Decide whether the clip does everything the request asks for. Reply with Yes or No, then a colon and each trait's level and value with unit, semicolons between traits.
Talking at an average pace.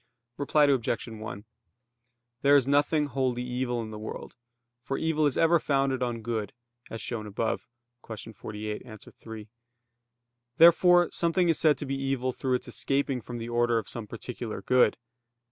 Yes: average, 160 wpm